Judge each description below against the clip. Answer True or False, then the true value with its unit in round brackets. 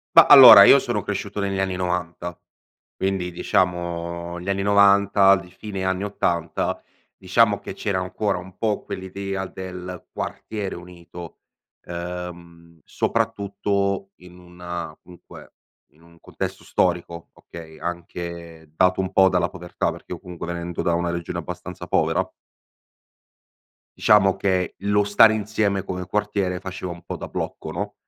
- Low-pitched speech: True (90 Hz)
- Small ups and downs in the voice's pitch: True (2.1 semitones)